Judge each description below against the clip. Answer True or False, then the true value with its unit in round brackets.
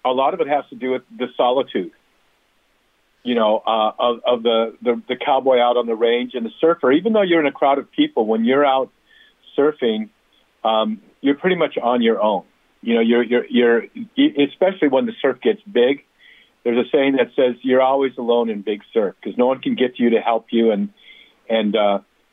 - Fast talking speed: True (215 wpm)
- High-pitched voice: False (125 Hz)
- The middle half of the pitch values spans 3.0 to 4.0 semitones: True (3.7 semitones)